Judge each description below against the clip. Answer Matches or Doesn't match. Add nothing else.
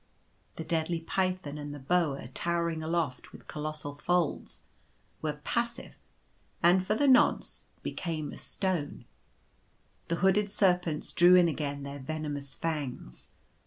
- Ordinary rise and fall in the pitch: Matches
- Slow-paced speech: Matches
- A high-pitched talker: Doesn't match